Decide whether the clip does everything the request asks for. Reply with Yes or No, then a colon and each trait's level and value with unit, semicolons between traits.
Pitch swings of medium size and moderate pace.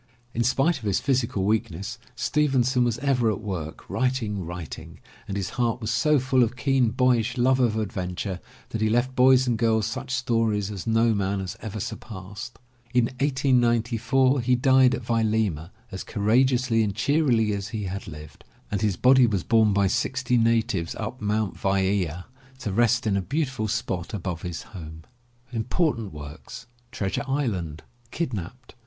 Yes: average, 4.2 semitones; average, 160 wpm